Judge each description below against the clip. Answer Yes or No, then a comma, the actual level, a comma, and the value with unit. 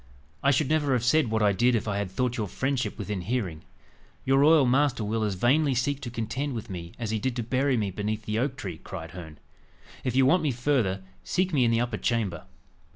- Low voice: Yes, low, 120 Hz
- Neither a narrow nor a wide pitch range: Yes, average, 4.5 semitones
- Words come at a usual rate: No, fast, 230 wpm